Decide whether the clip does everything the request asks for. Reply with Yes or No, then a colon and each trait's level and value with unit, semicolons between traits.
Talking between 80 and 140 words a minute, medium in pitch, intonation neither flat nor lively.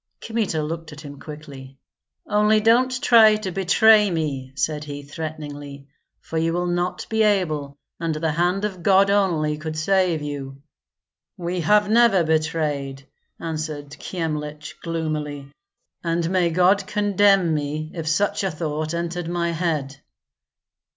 Yes: slow, 135 wpm; medium, 165 Hz; average, 4.1 semitones